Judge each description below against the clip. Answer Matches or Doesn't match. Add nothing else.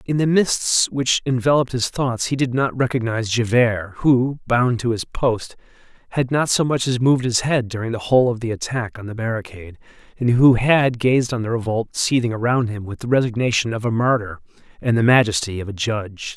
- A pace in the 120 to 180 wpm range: Doesn't match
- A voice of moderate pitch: Doesn't match